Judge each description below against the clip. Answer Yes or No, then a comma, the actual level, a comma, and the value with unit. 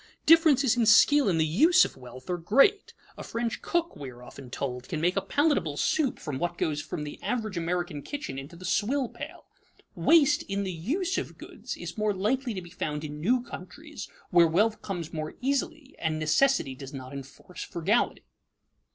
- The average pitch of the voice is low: No, medium, 185 Hz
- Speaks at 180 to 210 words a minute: Yes, average, 190 wpm